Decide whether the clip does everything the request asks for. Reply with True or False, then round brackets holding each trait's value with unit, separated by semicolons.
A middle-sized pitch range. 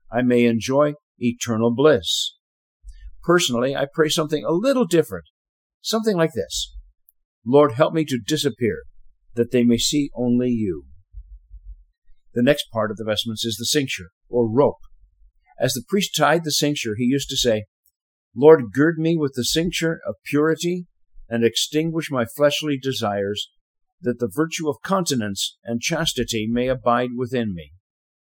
False (6.2 semitones)